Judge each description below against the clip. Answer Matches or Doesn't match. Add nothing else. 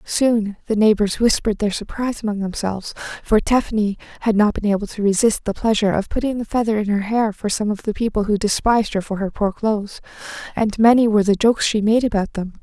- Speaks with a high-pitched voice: Matches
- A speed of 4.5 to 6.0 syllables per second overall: Doesn't match